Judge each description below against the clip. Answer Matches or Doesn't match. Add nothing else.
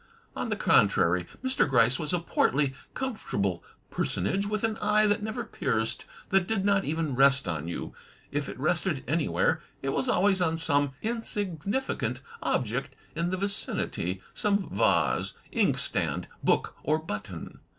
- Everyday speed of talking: Matches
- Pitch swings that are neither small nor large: Doesn't match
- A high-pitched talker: Doesn't match